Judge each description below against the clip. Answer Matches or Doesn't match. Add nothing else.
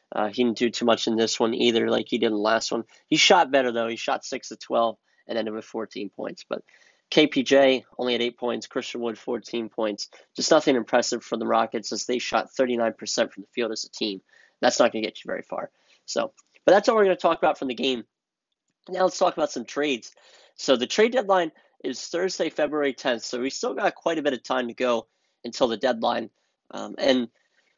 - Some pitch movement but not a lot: Matches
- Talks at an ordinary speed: Doesn't match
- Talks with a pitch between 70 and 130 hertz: Matches